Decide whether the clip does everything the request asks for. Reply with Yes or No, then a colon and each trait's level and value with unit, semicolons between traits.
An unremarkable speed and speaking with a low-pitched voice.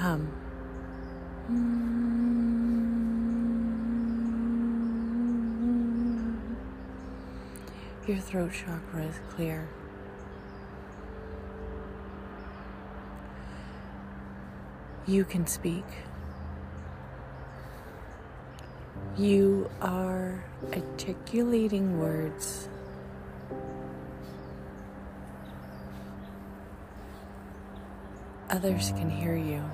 No: slow, 35 wpm; low, 100 Hz